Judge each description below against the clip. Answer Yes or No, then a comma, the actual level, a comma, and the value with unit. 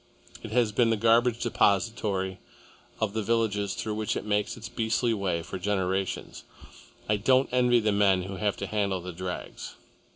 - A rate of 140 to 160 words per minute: No, average, 170 wpm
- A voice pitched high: No, low, 105 Hz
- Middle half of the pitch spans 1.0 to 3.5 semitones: Yes, average, 2.9 semitones